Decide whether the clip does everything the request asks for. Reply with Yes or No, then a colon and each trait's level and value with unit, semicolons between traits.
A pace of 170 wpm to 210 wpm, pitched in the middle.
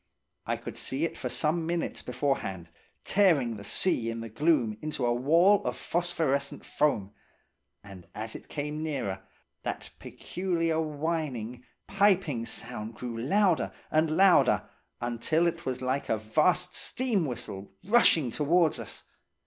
No: average, 140 wpm; medium, 150 Hz